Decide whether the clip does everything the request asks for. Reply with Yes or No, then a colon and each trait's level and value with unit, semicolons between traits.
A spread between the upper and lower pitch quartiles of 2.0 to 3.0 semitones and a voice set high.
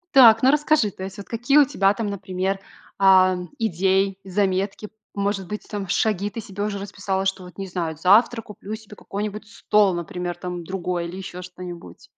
Yes: narrow, 2.4 semitones; high, 195 Hz